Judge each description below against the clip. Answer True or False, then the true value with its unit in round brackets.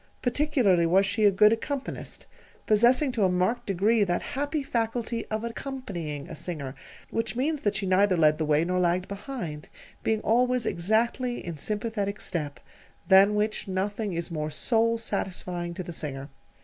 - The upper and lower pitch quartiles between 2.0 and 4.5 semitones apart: False (4.9 semitones)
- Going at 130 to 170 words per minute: True (160 wpm)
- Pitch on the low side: False (205 Hz)